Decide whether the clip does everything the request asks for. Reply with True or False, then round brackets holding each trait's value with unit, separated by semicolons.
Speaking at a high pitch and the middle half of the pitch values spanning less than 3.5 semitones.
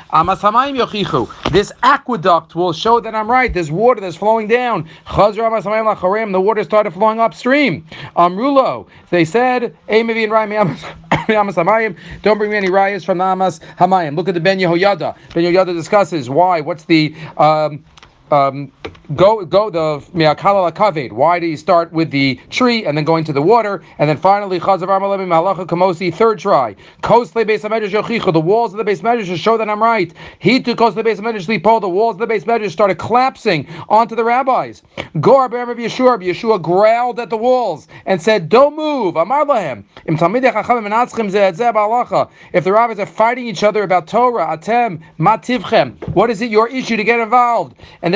False (210 Hz; 4.6 semitones)